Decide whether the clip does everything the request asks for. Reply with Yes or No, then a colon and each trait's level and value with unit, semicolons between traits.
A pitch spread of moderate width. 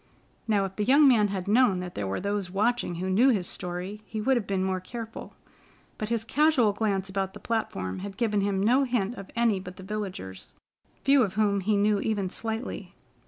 Yes: average, 3.0 semitones